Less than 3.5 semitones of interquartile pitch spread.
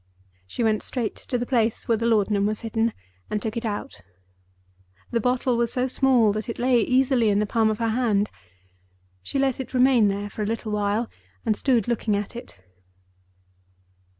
Yes: narrow, 2.6 semitones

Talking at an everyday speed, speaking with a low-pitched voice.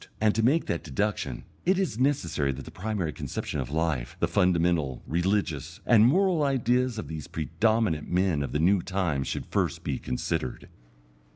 Yes: average, 170 wpm; very low, 90 Hz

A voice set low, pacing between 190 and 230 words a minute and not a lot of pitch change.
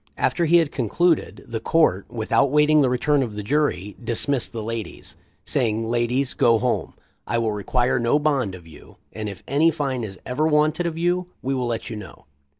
No: low, 125 Hz; average, 195 wpm; average, 5.1 semitones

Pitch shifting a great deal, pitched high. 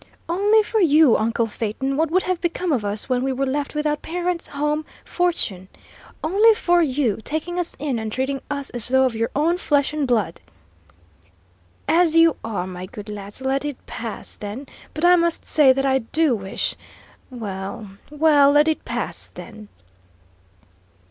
Yes: wide, 6.1 semitones; very high, 280 Hz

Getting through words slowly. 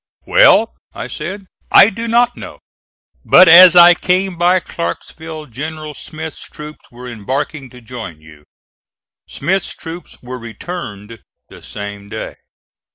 Yes: slow, 130 wpm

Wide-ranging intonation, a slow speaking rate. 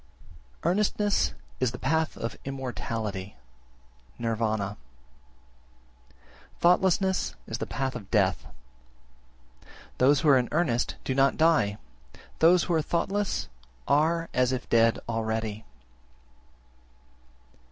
Yes: wide, 6.6 semitones; slow, 100 wpm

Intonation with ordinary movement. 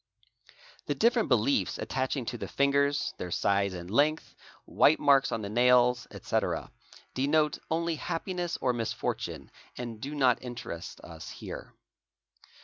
Yes: average, 4.1 semitones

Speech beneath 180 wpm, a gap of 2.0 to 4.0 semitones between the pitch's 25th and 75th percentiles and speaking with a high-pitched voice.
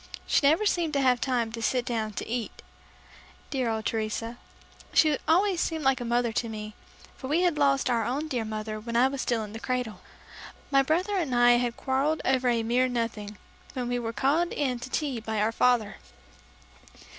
No: average, 200 wpm; average, 3.5 semitones; high, 245 Hz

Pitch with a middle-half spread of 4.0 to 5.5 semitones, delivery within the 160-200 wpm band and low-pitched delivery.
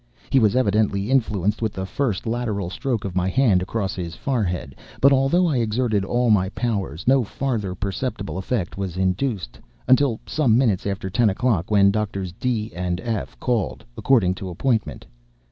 Yes: average, 4.6 semitones; average, 165 wpm; low, 105 Hz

